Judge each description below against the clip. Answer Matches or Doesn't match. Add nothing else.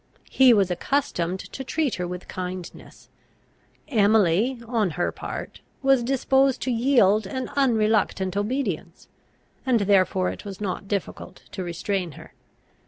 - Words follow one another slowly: Matches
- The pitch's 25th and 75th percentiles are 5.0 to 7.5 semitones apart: Matches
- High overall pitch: Matches